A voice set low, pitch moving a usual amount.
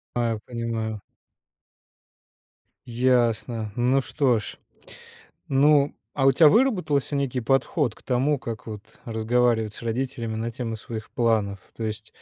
Yes: low, 120 Hz; average, 3.2 semitones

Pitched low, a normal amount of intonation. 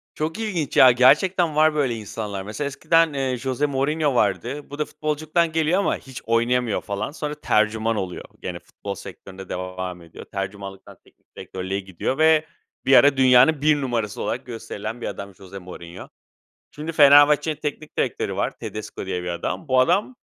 No: low, 130 Hz; wide, 7.0 semitones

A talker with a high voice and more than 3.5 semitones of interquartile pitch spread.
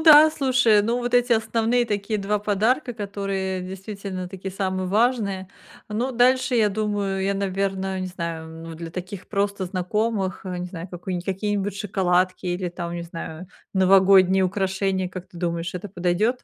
No: high, 195 Hz; narrow, 2.5 semitones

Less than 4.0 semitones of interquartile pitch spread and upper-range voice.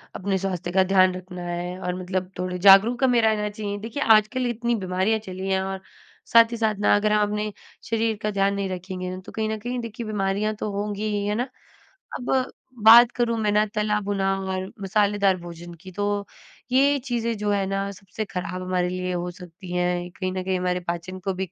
Yes: average, 2.8 semitones; high, 200 Hz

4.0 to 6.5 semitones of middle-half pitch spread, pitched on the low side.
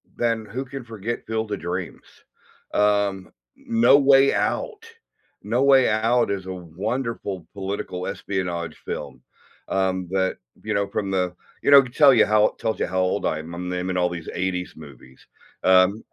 Yes: average, 4.3 semitones; low, 100 Hz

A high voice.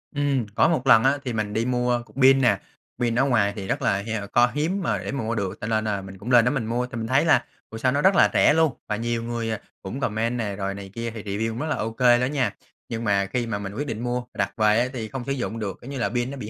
No: low, 115 Hz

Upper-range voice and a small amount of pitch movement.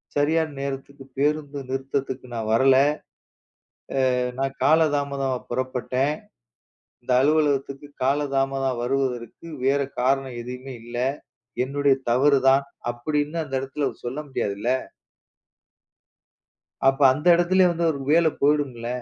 No: low, 135 Hz; narrow, 2.0 semitones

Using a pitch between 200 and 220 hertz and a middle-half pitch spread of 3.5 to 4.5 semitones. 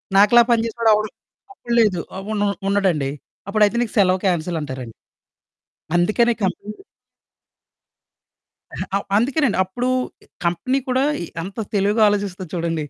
Yes: high, 205 Hz; average, 4.1 semitones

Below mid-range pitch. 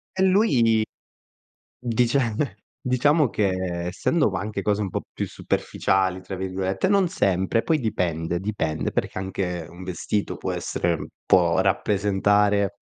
Yes: low, 100 Hz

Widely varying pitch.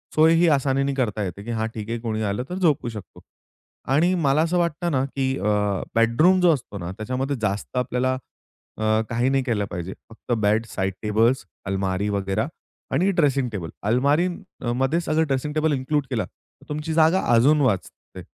Yes: wide, 5.9 semitones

